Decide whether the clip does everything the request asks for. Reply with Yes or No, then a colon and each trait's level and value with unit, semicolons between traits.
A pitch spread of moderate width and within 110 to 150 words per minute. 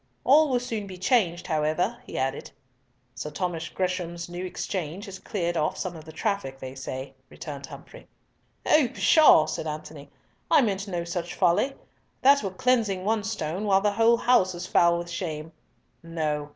No: average, 4.7 semitones; average, 165 wpm